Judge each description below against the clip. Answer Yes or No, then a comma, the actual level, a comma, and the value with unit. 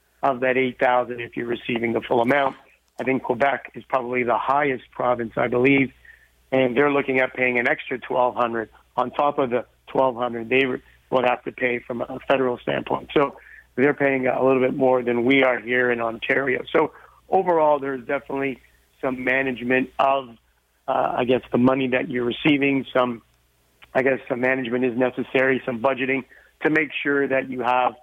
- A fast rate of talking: No, average, 185 wpm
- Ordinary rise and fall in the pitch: No, narrow, 1.5 semitones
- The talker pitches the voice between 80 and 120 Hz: No, low, 130 Hz